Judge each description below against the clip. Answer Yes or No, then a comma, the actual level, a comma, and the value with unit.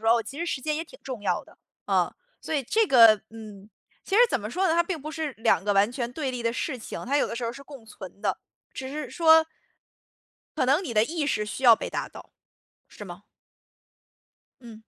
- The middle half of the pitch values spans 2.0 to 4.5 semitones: No, wide, 5.6 semitones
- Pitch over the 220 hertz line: Yes, very high, 255 Hz